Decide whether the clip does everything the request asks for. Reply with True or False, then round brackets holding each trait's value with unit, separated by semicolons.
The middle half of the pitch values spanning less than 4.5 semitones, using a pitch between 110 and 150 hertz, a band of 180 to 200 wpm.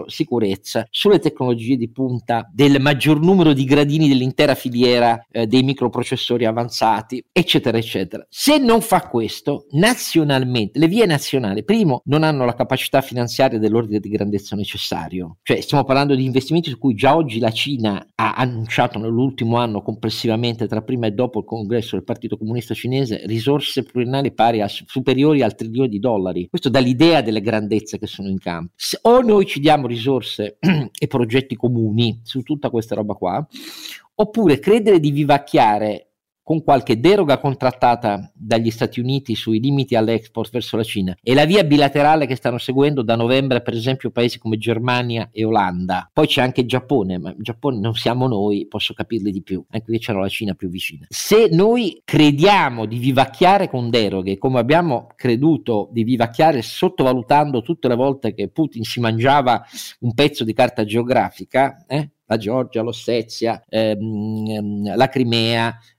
False (4.1 semitones; 120 Hz; 165 wpm)